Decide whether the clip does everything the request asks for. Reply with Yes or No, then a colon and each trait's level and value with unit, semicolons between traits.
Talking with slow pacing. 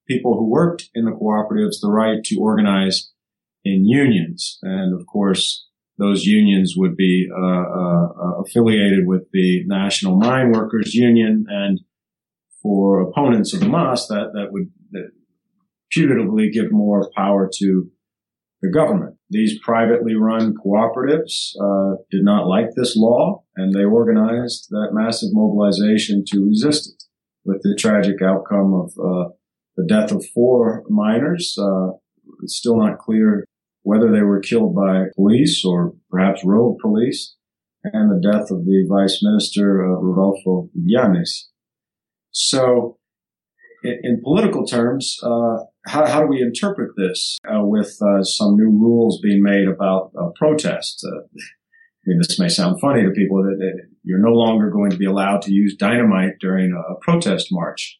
No: average, 155 wpm